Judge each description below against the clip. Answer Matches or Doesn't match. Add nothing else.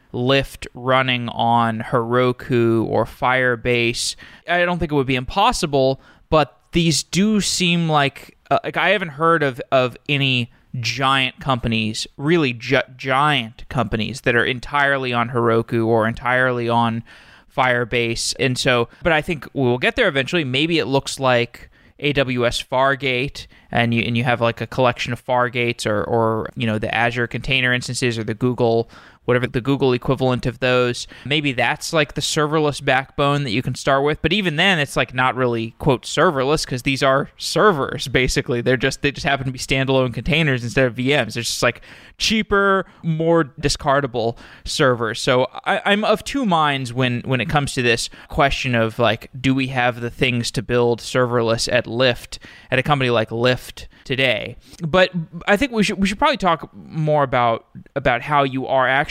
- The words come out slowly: Doesn't match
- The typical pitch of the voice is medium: Doesn't match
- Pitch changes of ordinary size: Matches